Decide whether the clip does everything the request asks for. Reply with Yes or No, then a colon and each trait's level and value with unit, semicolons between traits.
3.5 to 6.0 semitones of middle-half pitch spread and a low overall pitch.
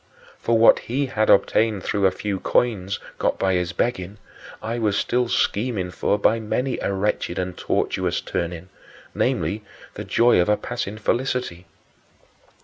Yes: average, 3.9 semitones; low, 105 Hz